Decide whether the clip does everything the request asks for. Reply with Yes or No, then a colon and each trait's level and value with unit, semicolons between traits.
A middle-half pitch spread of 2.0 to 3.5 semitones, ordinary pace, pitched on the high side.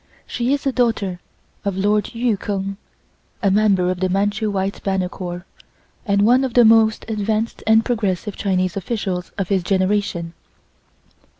Yes: average, 2.8 semitones; average, 155 wpm; high, 200 Hz